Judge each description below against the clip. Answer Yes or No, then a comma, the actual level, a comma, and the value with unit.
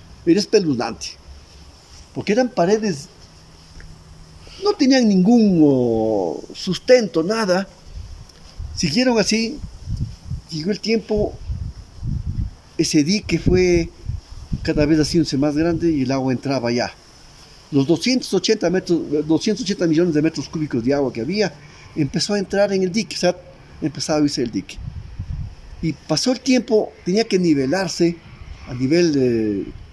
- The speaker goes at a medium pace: Yes, average, 125 wpm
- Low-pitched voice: No, medium, 155 Hz